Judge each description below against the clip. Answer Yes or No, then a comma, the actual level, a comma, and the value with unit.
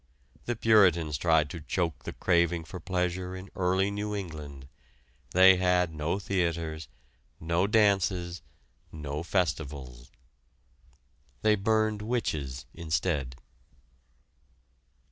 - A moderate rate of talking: No, slow, 100 wpm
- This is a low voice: Yes, very low, 90 Hz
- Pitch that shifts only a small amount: No, average, 3.7 semitones